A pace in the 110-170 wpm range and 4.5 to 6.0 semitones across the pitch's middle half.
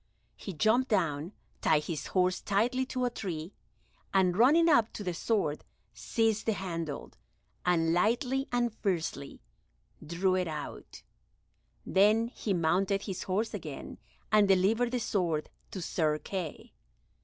Yes: slow, 135 wpm; average, 5.1 semitones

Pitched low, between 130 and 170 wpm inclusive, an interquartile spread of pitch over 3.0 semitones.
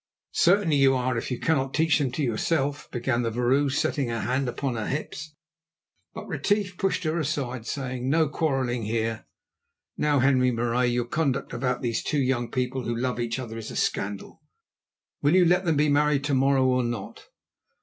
No: low, 130 Hz; average, 185 wpm; average, 3.6 semitones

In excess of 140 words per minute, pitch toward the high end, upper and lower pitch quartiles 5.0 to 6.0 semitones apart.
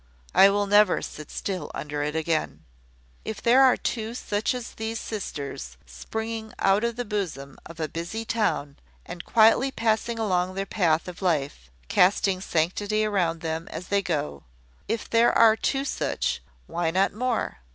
Yes: average, 160 wpm; high, 195 Hz; average, 5.3 semitones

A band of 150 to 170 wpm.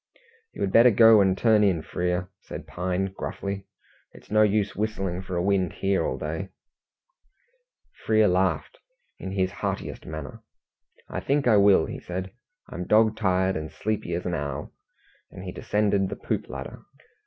Yes: average, 165 wpm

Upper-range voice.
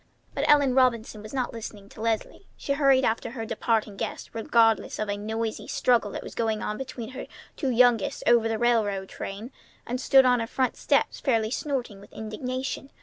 Yes: high, 230 Hz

